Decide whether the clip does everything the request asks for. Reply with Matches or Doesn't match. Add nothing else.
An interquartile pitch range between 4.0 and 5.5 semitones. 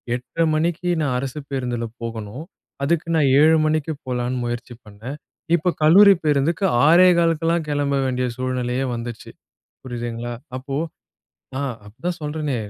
Matches